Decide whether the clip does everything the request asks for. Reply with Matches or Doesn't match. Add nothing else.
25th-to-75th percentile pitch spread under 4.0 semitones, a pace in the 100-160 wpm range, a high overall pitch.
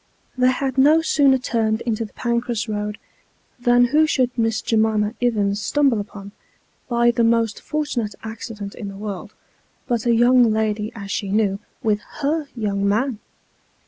Matches